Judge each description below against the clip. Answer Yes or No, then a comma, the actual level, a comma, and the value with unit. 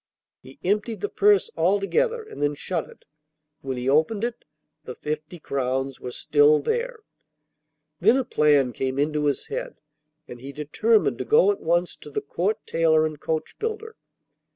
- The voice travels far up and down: Yes, wide, 7.5 semitones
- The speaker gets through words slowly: No, average, 160 wpm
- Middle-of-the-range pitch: Yes, medium, 160 Hz